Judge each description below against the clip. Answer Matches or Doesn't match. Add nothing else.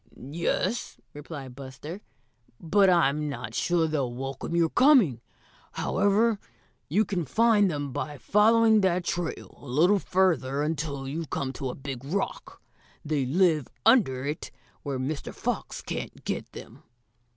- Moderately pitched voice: Matches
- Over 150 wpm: Doesn't match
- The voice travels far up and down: Matches